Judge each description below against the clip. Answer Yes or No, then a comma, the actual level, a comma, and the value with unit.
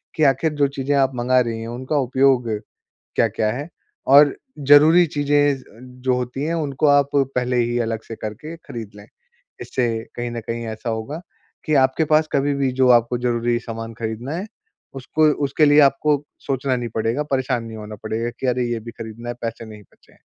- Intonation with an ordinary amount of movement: Yes, average, 3.4 semitones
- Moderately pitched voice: No, low, 125 Hz